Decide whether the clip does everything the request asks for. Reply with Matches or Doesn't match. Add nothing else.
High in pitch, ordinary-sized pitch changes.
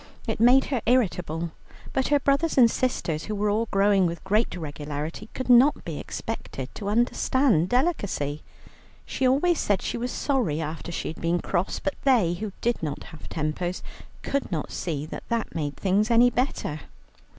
Doesn't match